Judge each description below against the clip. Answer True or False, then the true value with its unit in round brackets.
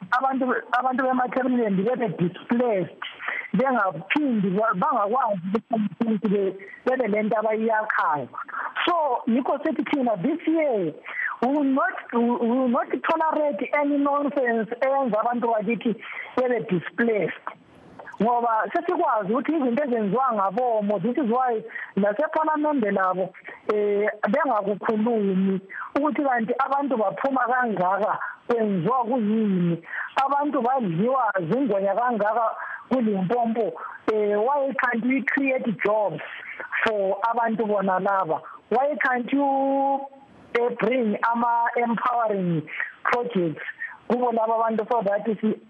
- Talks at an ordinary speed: False (90 wpm)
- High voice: True (235 Hz)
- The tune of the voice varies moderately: True (4.1 semitones)